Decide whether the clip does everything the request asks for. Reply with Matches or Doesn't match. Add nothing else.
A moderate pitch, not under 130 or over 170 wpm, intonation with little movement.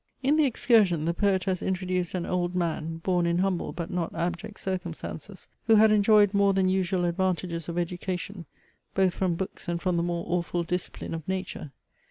Doesn't match